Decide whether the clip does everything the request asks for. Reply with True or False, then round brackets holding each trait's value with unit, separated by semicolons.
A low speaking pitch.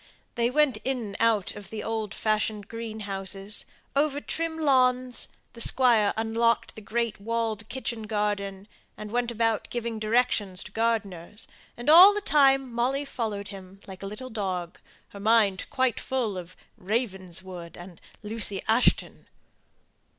False (220 Hz)